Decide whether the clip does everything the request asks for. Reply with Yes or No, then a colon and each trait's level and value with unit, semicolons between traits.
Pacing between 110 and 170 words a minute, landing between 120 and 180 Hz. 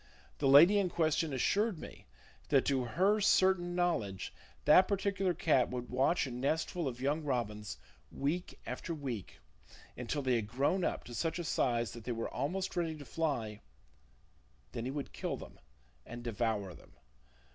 Yes: average, 165 wpm; medium, 140 Hz